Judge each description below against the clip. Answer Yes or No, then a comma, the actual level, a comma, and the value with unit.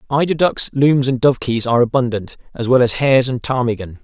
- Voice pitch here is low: Yes, low, 125 Hz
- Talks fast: No, average, 195 wpm